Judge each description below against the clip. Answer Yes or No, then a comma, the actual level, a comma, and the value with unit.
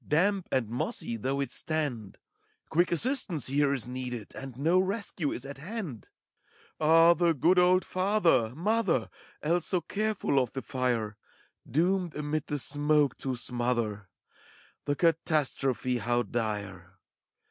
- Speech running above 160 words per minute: No, average, 145 wpm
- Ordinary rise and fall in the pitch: No, wide, 5.8 semitones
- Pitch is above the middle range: No, medium, 145 Hz